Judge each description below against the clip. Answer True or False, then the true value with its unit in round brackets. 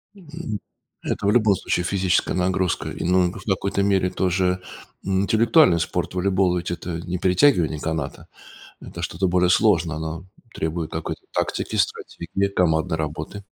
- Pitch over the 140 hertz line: False (90 Hz)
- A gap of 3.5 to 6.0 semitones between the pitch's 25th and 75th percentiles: False (2.6 semitones)